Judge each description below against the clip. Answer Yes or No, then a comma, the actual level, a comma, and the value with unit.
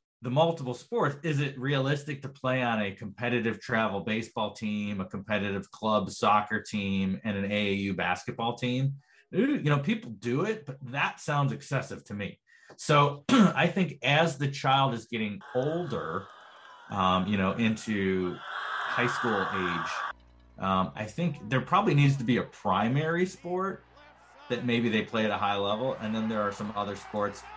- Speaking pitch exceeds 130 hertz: No, low, 120 Hz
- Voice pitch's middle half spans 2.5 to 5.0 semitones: No, wide, 5.6 semitones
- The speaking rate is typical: Yes, average, 170 wpm